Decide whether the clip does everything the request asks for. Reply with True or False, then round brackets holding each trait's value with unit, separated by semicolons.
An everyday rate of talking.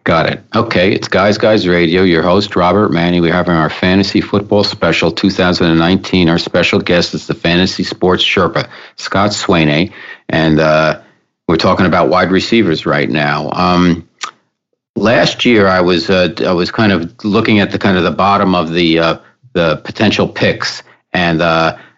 True (170 wpm)